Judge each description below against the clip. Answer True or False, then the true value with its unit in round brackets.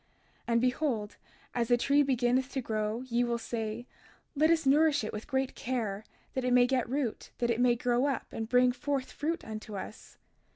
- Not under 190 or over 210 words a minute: True (200 wpm)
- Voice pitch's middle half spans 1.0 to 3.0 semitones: True (2.7 semitones)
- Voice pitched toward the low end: False (245 Hz)